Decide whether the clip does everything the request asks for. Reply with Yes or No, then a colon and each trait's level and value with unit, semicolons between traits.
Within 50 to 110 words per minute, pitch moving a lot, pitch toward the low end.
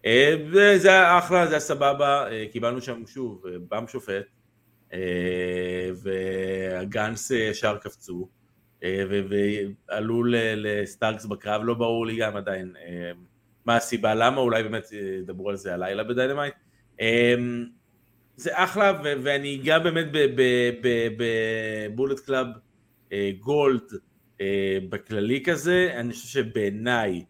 No: average, 105 wpm; average, 4.3 semitones; low, 115 Hz